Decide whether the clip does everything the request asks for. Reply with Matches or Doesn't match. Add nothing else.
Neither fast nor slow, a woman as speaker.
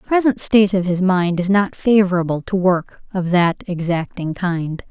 Matches